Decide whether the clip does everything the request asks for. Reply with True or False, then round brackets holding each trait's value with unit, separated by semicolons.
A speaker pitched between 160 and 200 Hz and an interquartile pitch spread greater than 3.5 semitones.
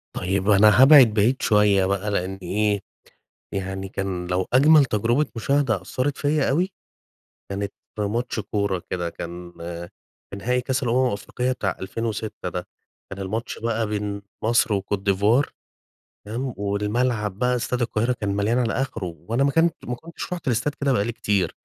False (105 Hz; 4.1 semitones)